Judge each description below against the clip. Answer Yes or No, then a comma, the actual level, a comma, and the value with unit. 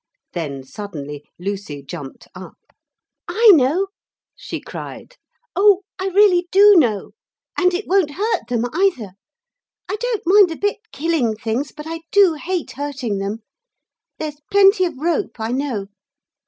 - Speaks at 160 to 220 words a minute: No, average, 140 wpm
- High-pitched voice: Yes, very high, 300 Hz